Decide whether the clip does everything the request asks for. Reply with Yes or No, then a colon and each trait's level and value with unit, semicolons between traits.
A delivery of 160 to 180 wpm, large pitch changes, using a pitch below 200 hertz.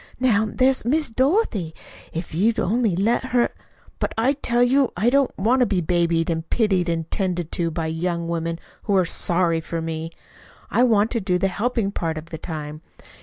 No: average, 195 wpm; wide, 6.2 semitones; medium, 185 Hz